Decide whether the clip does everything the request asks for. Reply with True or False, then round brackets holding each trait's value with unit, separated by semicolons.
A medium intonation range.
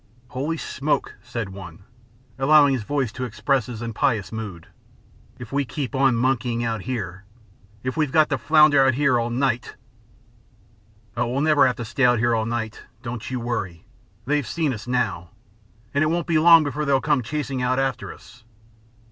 True (3.7 semitones)